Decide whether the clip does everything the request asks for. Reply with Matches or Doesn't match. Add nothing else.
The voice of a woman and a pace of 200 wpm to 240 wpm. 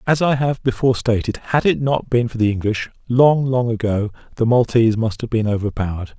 Doesn't match